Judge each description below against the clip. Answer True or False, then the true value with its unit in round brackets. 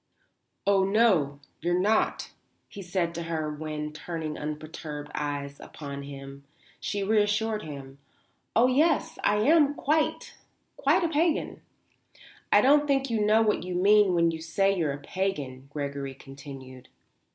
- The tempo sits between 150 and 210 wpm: False (140 wpm)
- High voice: False (170 Hz)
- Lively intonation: True (6.7 semitones)